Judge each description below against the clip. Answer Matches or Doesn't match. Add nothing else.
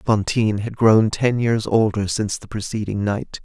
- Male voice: Matches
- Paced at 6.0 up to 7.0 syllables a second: Doesn't match